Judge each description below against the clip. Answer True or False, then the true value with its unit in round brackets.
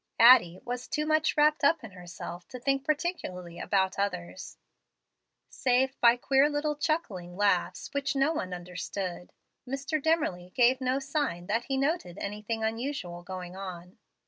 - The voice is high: True (235 Hz)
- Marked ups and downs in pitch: True (7.6 semitones)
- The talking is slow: False (150 wpm)